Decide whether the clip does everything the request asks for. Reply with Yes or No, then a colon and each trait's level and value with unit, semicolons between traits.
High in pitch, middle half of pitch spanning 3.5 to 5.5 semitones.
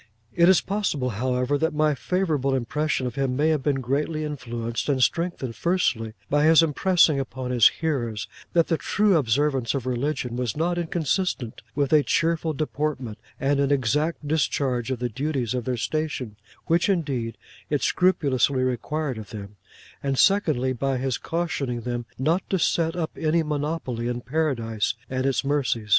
No: medium, 140 Hz; average, 4.2 semitones